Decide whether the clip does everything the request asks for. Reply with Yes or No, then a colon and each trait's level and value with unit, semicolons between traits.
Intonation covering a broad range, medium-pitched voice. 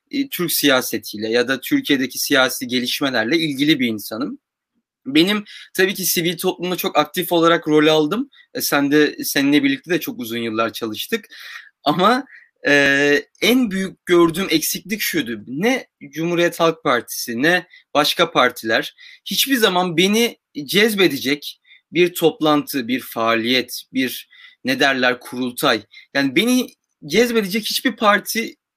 Yes: wide, 7.1 semitones; medium, 165 Hz